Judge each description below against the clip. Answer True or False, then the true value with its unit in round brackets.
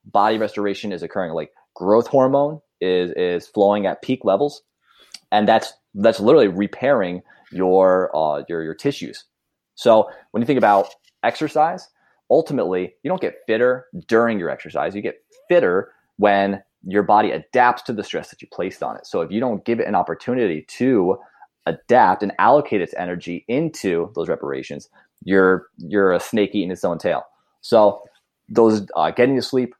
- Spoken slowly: False (165 wpm)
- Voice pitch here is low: True (105 Hz)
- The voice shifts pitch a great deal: True (6.1 semitones)